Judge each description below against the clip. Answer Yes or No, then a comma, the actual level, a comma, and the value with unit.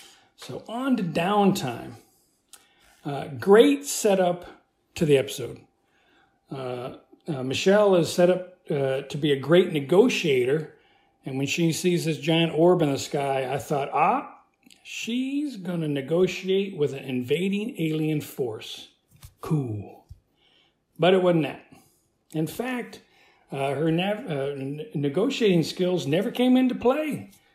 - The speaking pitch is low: No, medium, 175 Hz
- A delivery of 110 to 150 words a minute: Yes, slow, 135 wpm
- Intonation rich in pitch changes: Yes, wide, 6.9 semitones